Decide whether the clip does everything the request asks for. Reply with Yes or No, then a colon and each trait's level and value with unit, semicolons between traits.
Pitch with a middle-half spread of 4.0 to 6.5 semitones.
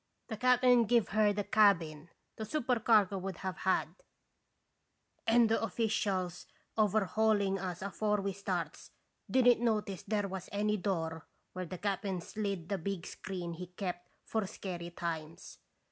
No: average, 3.2 semitones